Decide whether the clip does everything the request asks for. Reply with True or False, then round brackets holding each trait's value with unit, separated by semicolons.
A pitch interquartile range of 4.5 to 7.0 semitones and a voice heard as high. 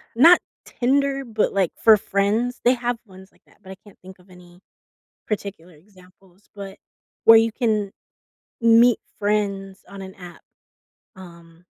False (3.4 semitones; 200 Hz)